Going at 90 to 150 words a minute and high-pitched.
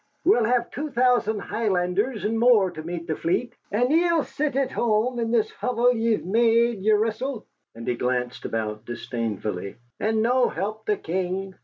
No: average, 165 wpm; high, 220 Hz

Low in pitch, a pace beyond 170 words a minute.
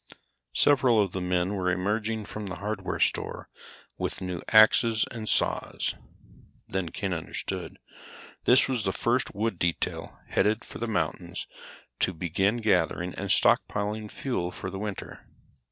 No: low, 100 Hz; average, 140 wpm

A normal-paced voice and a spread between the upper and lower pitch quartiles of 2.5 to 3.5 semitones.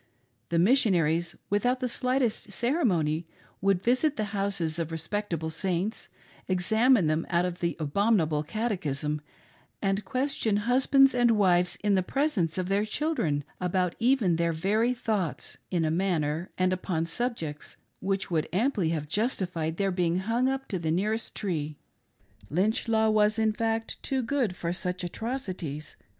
No: average, 150 wpm; average, 5.1 semitones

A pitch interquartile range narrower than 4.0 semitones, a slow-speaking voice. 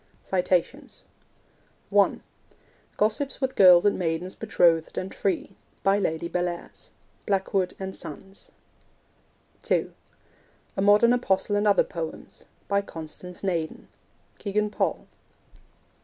Yes: average, 2.9 semitones; slow, 100 wpm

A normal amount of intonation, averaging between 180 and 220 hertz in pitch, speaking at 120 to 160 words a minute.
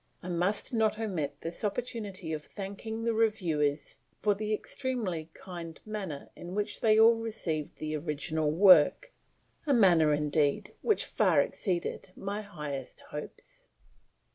No: wide, 5.8 semitones; high, 190 Hz; slow, 135 wpm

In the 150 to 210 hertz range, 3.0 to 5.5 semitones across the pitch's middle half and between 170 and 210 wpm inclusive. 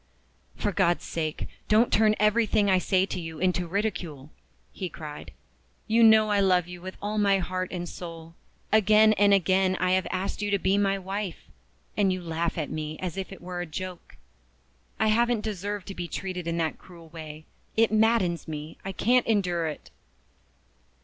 Yes: medium, 185 Hz; average, 3.3 semitones; average, 185 wpm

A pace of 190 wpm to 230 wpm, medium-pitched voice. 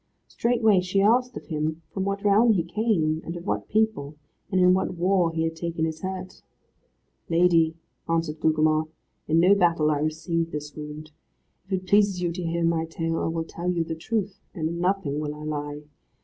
Yes: average, 195 wpm; medium, 170 Hz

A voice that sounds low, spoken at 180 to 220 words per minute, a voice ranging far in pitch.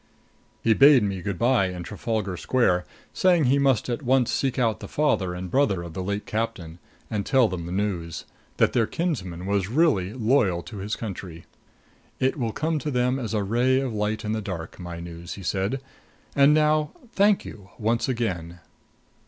Yes: low, 110 Hz; average, 190 wpm; wide, 6.0 semitones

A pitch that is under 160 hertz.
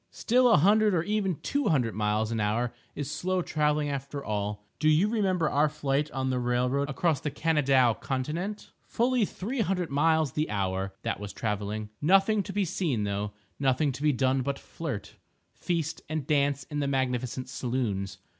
Yes: medium, 140 Hz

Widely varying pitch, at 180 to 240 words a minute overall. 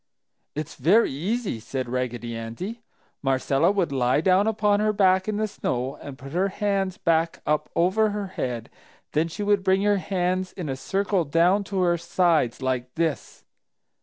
No: wide, 6.6 semitones; average, 170 wpm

